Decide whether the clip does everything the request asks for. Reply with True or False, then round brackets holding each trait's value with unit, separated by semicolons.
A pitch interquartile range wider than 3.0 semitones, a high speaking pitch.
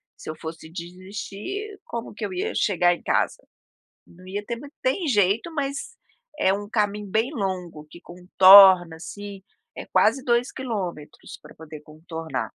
True (4.8 semitones; 195 Hz)